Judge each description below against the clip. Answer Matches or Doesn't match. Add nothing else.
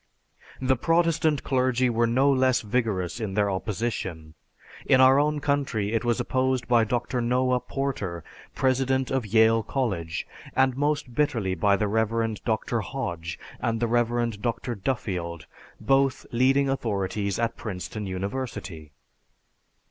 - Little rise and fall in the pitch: Doesn't match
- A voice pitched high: Doesn't match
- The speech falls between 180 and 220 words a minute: Doesn't match